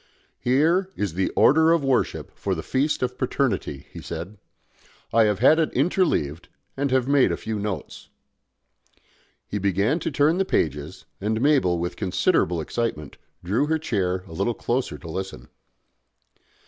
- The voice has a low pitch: Yes, low, 110 Hz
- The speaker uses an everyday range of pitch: No, wide, 7.7 semitones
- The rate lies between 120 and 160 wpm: Yes, average, 155 wpm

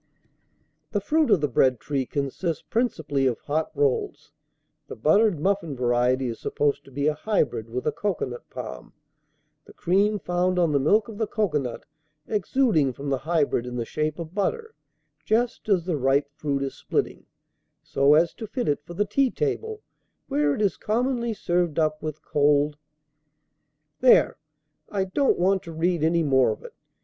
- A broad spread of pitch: Yes, wide, 6.3 semitones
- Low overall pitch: No, medium, 155 Hz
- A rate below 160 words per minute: No, average, 175 wpm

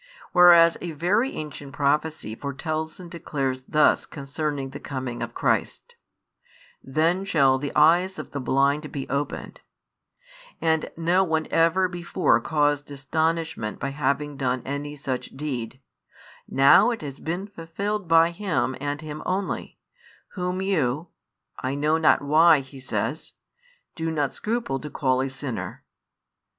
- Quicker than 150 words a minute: No, average, 140 wpm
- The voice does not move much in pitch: No, average, 3.4 semitones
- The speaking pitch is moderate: Yes, medium, 150 Hz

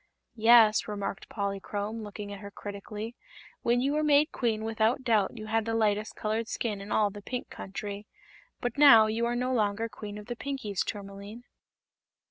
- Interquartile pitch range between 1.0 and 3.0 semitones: Yes, narrow, 2.5 semitones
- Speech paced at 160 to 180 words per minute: Yes, average, 175 wpm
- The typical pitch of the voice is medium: No, high, 220 Hz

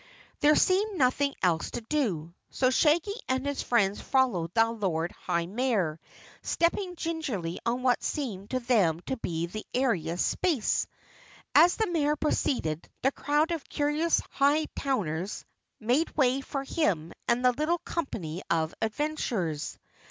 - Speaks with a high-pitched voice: Yes, very high, 255 Hz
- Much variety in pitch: Yes, wide, 8.5 semitones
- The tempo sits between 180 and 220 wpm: No, average, 140 wpm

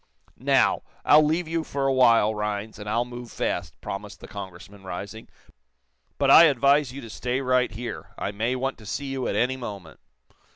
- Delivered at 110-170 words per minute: No, average, 190 wpm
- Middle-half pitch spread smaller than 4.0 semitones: No, average, 4.3 semitones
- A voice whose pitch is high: No, low, 120 Hz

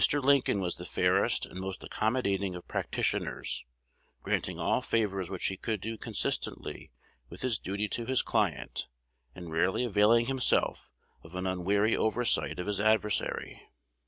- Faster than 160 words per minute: No, average, 145 wpm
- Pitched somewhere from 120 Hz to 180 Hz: No, low, 105 Hz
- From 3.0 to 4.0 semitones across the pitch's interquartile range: Yes, average, 3.6 semitones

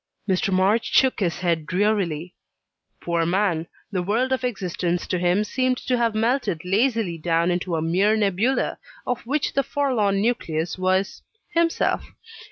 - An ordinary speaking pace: Yes, average, 150 wpm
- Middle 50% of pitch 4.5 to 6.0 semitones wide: Yes, average, 5.1 semitones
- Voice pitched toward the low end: No, high, 195 Hz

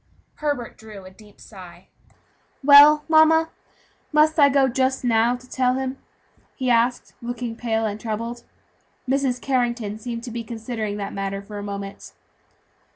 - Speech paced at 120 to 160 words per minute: Yes, average, 150 wpm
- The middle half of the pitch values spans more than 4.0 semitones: No, average, 3.7 semitones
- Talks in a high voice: Yes, high, 240 Hz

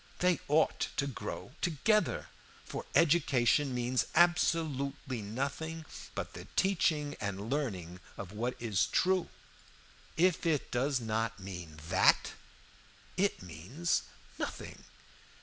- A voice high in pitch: No, medium, 140 Hz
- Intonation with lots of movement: Yes, wide, 6.9 semitones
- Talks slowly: Yes, slow, 110 wpm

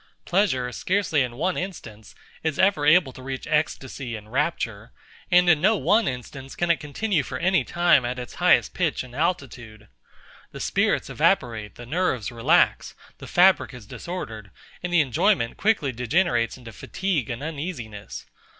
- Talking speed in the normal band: Yes, average, 160 wpm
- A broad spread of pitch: Yes, wide, 6.6 semitones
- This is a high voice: No, medium, 140 Hz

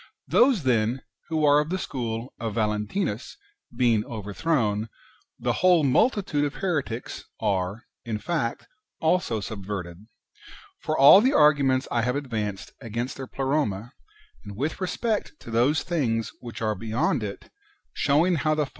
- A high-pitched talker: No, low, 125 Hz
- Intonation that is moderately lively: No, wide, 5.9 semitones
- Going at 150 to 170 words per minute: No, average, 140 wpm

